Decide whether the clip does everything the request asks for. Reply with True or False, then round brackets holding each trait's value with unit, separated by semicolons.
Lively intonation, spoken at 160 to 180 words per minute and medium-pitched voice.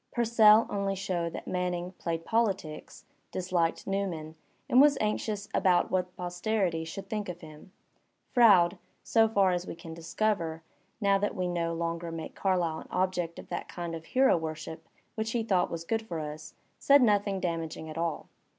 False (3.6 semitones; 170 wpm; 180 Hz)